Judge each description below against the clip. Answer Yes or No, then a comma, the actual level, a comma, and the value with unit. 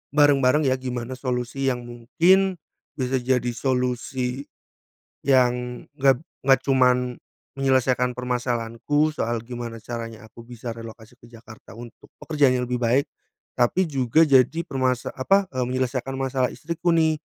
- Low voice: Yes, low, 125 Hz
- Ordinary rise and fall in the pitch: No, narrow, 2.0 semitones